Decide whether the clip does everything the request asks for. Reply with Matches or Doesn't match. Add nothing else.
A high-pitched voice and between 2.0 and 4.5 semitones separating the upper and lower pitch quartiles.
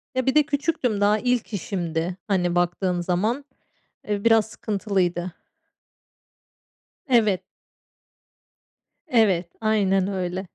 Matches